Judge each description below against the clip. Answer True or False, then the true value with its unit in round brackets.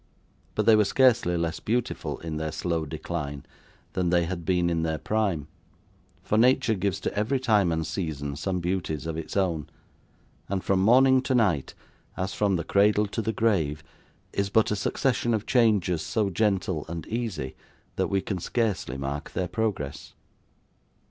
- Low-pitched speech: True (95 Hz)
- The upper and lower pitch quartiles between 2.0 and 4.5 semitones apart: False (4.9 semitones)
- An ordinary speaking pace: True (170 wpm)